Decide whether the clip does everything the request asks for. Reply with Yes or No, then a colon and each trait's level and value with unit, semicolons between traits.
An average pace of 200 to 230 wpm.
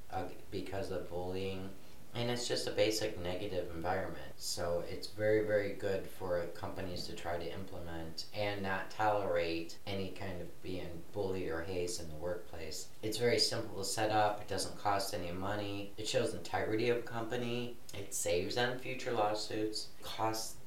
No: average, 170 wpm